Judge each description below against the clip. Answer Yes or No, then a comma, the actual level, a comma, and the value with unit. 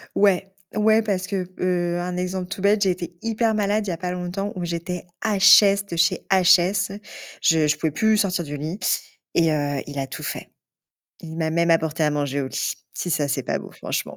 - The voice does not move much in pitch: No, average, 3.4 semitones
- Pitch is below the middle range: No, medium, 180 Hz